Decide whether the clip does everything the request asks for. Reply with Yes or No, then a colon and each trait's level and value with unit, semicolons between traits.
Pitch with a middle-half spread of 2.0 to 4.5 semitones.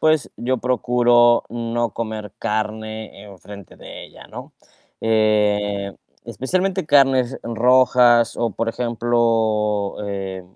Yes: narrow, 2.4 semitones